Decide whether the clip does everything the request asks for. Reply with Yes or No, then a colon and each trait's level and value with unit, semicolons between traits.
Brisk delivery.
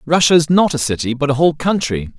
Yes: fast, 245 wpm